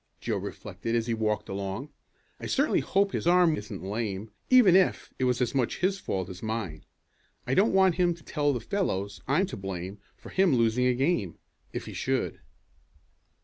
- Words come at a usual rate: Yes, average, 190 wpm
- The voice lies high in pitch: No, low, 125 Hz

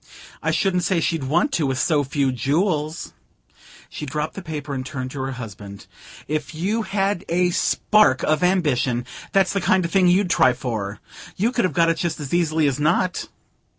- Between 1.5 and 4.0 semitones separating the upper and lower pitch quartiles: No, average, 5.2 semitones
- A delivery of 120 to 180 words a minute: No, average, 195 wpm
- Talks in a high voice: No, medium, 155 Hz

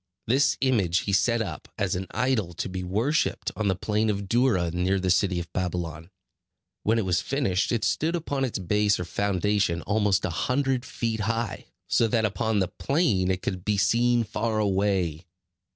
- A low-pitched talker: Yes, low, 105 Hz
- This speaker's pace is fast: No, average, 185 wpm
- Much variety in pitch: No, average, 4.1 semitones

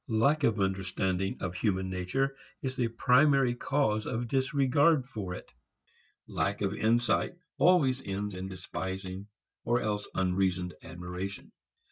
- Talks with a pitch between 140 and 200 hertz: No, low, 105 Hz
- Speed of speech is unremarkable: No, slow, 125 wpm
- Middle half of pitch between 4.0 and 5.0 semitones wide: No, wide, 5.5 semitones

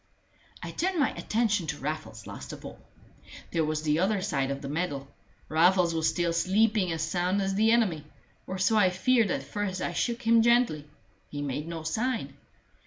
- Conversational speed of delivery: Yes, average, 185 wpm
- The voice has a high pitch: No, medium, 180 Hz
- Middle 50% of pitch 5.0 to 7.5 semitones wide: Yes, wide, 5.6 semitones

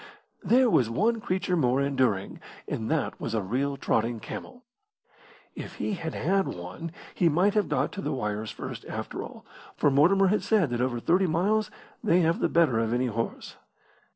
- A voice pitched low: No, medium, 155 Hz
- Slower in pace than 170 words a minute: No, average, 180 wpm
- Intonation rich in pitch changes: Yes, wide, 8.3 semitones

